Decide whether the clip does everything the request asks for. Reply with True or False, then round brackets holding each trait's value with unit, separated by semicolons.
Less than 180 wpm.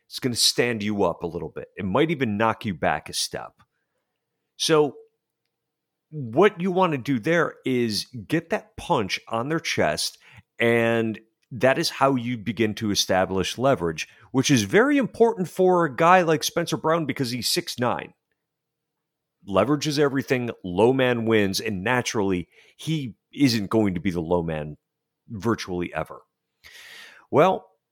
True (155 wpm)